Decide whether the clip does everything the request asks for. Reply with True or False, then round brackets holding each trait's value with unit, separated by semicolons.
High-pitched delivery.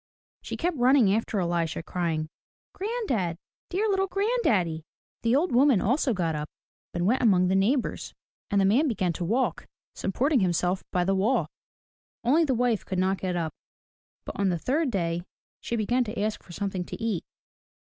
True (205 Hz)